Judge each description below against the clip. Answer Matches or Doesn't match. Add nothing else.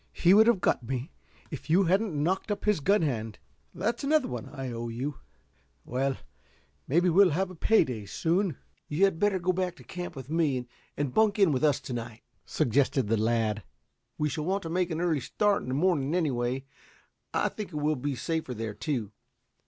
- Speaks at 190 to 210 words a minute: Matches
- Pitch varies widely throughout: Matches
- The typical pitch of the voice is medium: Matches